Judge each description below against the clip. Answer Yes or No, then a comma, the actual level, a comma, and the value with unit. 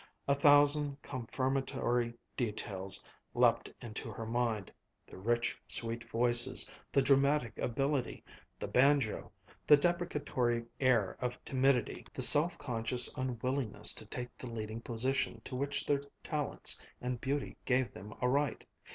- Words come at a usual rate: No, slow, 130 wpm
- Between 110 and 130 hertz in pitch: Yes, low, 125 Hz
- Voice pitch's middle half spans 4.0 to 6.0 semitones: No, average, 3.1 semitones